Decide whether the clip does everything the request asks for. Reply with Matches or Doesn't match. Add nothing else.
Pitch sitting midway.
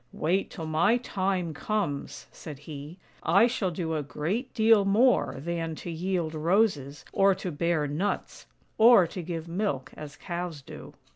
Matches